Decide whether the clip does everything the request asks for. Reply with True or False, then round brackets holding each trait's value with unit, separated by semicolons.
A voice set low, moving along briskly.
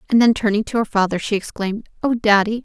False (215 Hz; 225 wpm)